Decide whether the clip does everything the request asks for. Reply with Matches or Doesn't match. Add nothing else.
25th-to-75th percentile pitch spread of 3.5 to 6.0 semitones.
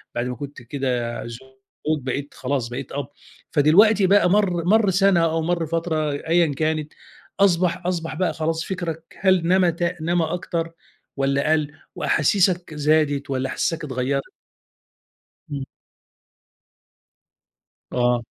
Matches